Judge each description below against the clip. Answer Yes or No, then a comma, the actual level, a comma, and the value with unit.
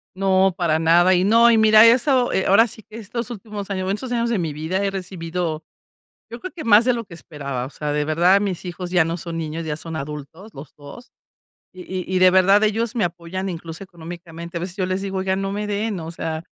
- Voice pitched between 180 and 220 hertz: Yes, medium, 185 Hz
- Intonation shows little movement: No, average, 4.1 semitones